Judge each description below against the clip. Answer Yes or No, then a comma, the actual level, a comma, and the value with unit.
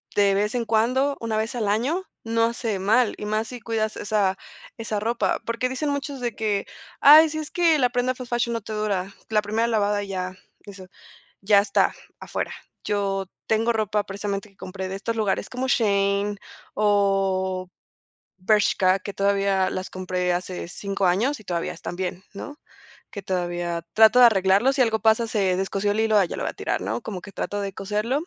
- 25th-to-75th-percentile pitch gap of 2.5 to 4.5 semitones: Yes, average, 2.9 semitones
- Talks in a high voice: Yes, high, 210 Hz